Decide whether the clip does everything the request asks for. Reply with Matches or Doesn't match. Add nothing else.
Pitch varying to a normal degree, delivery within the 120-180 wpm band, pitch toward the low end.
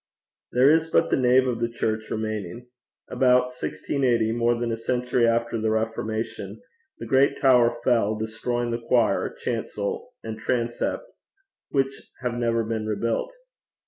Doesn't match